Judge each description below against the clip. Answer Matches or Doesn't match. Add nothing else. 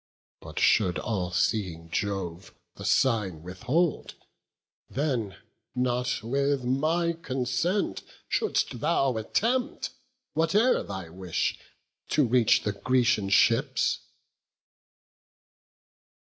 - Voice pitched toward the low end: Matches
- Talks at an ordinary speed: Doesn't match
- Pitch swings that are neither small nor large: Doesn't match